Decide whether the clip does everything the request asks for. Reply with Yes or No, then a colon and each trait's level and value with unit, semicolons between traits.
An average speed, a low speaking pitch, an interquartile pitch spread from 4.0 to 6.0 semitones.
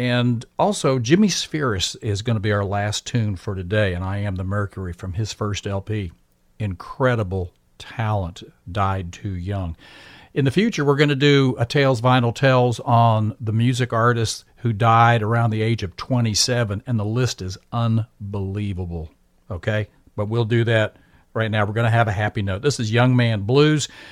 No: average, 180 wpm; low, 110 Hz; average, 3.5 semitones